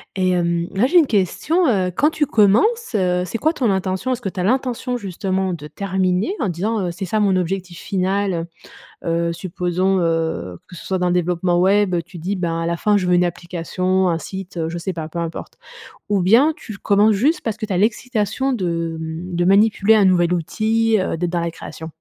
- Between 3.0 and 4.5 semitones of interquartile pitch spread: Yes, average, 3.5 semitones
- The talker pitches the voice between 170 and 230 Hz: Yes, medium, 185 Hz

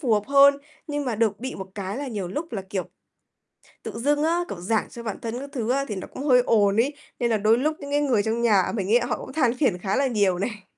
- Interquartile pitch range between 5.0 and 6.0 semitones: Yes, average, 5.3 semitones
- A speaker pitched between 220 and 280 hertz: Yes, high, 235 Hz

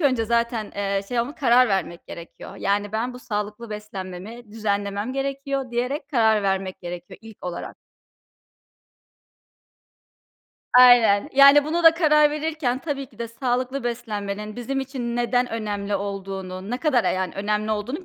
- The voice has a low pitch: No, high, 230 Hz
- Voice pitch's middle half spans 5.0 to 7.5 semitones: No, average, 4.2 semitones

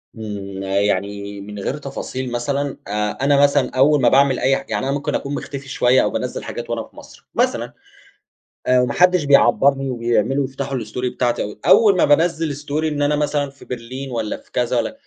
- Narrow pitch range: No, average, 3.4 semitones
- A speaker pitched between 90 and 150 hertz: Yes, low, 135 Hz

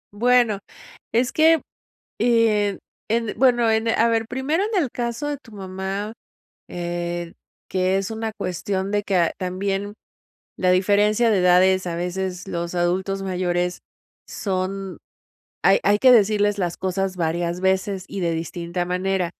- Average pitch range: Yes, average, 3.5 semitones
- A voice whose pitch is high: Yes, high, 195 Hz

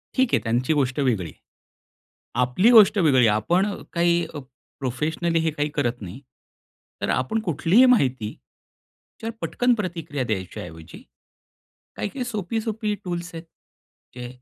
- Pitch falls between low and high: Yes, medium, 160 Hz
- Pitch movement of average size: No, wide, 8.6 semitones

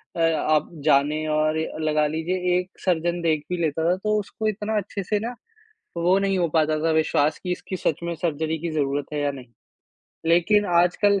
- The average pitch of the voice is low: No, medium, 165 Hz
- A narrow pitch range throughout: No, average, 3.1 semitones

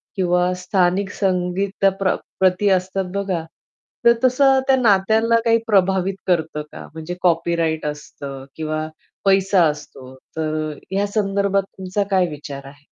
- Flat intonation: No, average, 3.7 semitones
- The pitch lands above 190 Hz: No, medium, 185 Hz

